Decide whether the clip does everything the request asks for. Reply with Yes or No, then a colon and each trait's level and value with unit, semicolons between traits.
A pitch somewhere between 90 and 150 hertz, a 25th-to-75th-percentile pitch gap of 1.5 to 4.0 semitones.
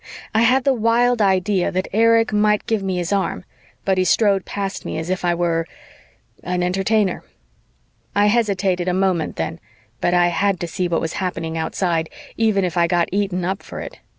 No: high, 190 Hz; average, 3.0 semitones